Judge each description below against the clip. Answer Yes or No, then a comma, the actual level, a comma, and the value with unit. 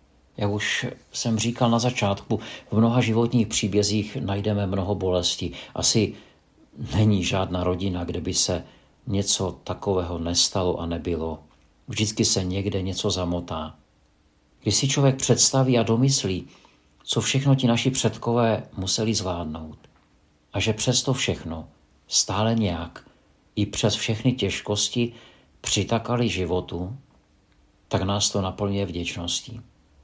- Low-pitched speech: Yes, low, 100 Hz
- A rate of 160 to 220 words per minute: No, average, 120 wpm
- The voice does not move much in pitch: No, average, 4.6 semitones